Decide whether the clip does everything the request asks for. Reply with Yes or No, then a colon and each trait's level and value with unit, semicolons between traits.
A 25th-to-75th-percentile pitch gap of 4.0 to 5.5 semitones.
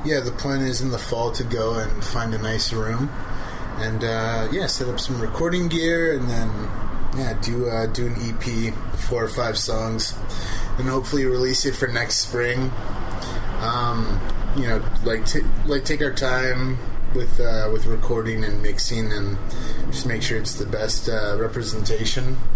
No: average, 2.8 semitones